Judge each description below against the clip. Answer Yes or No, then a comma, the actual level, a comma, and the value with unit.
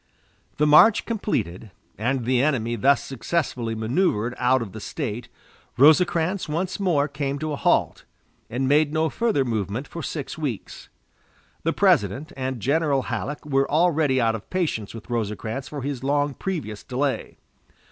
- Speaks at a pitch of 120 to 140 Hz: Yes, low, 135 Hz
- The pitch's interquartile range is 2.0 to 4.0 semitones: No, average, 4.8 semitones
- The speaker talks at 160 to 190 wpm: No, average, 150 wpm